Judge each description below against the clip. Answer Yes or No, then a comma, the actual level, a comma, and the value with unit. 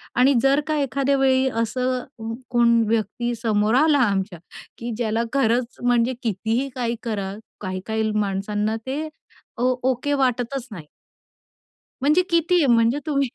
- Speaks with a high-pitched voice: Yes, high, 240 Hz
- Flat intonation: No, average, 3.5 semitones